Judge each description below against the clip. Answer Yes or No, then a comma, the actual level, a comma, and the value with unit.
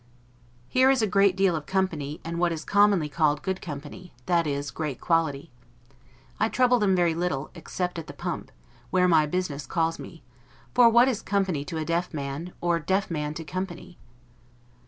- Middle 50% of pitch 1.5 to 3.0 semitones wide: No, average, 3.7 semitones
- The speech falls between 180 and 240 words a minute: Yes, average, 185 wpm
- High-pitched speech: No, medium, 170 Hz